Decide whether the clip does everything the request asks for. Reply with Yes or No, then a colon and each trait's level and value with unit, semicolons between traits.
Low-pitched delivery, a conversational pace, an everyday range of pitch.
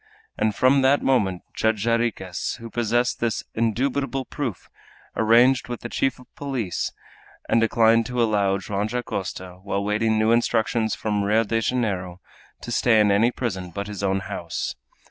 Yes: low, 110 Hz; average, 160 wpm; average, 3.2 semitones